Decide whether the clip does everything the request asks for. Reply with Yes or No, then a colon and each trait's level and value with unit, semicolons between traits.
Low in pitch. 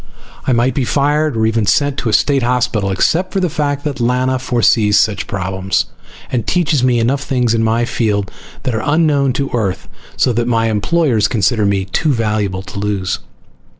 Yes: low, 120 Hz